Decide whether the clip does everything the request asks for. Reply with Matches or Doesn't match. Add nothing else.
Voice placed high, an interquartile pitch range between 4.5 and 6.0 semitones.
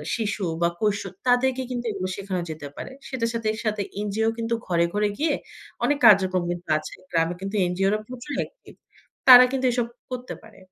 Matches